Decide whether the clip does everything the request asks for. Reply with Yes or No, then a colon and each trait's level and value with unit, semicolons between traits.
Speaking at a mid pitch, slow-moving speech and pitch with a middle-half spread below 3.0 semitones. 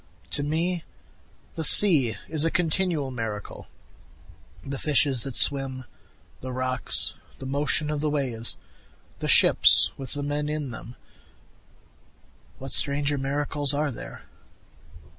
Yes: medium, 145 Hz; slow, 120 wpm; narrow, 2.5 semitones